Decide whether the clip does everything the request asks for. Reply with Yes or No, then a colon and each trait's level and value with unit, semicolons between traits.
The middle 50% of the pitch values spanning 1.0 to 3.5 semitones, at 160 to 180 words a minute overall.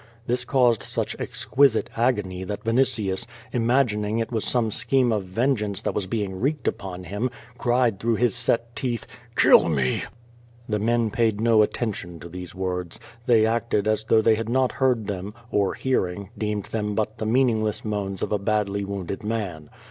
Yes: average, 3.0 semitones; average, 170 wpm